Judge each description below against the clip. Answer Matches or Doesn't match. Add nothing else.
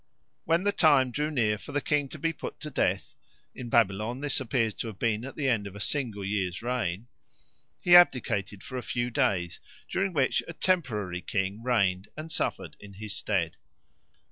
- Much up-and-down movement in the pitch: Matches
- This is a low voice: Matches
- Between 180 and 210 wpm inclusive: Matches